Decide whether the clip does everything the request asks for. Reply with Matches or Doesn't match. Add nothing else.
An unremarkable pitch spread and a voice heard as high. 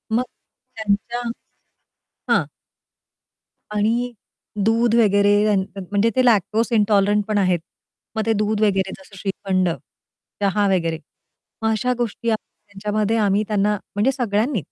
Doesn't match